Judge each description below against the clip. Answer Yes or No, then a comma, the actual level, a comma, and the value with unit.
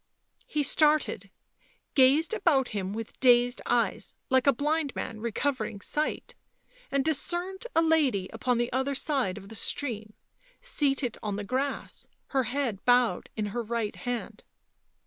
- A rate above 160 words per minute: No, average, 145 wpm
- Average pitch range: Yes, average, 4.4 semitones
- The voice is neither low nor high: No, very high, 255 Hz